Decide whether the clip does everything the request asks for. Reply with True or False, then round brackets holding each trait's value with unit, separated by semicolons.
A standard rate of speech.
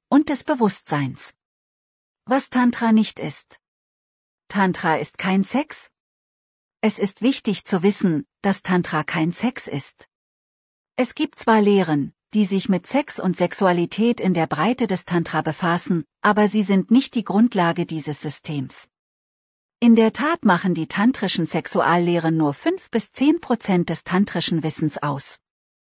True (140 wpm)